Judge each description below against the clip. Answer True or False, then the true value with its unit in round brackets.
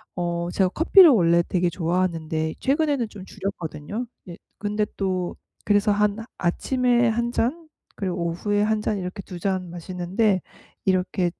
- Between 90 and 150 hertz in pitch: False (190 Hz)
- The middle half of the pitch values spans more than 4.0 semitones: False (3.7 semitones)